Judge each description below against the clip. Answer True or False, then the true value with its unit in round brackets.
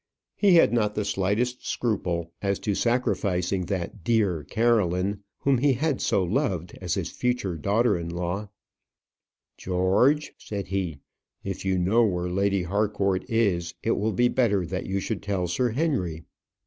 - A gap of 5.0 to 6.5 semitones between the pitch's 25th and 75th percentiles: False (4.5 semitones)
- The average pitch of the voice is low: True (100 Hz)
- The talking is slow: False (155 wpm)